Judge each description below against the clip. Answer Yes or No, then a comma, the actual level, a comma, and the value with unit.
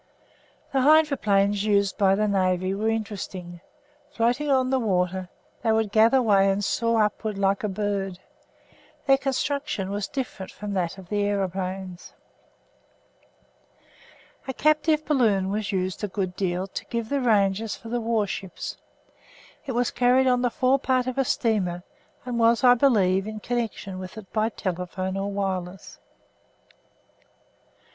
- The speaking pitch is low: No, high, 210 Hz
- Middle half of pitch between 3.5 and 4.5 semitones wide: Yes, average, 4.2 semitones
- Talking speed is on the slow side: No, average, 145 wpm